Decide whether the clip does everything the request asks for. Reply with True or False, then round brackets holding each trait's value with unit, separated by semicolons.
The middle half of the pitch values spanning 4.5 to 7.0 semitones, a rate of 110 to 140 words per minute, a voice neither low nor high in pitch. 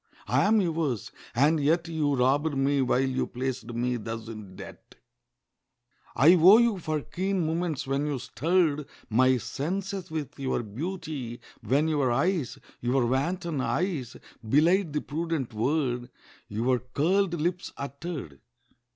True (4.9 semitones; 135 wpm; 145 Hz)